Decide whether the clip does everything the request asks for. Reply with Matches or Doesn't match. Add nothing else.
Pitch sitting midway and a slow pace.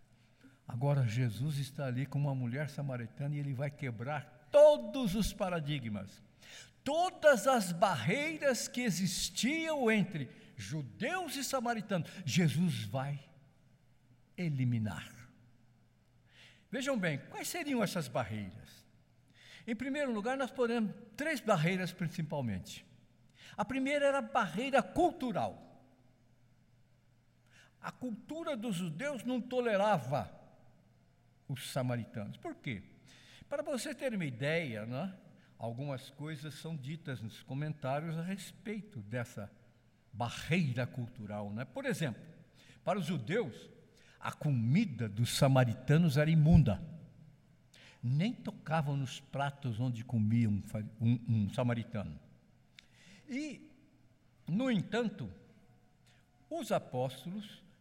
Matches